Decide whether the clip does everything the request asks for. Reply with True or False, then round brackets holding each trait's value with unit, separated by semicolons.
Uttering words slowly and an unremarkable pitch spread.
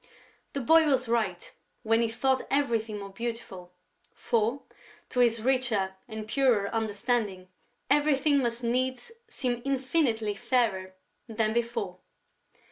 True (120 wpm; 3.3 semitones)